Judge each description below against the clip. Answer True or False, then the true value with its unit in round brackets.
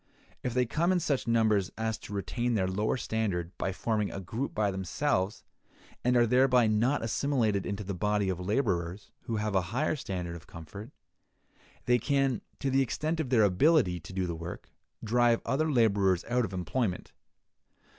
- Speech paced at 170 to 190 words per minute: True (175 wpm)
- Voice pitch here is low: True (110 Hz)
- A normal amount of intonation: True (4.7 semitones)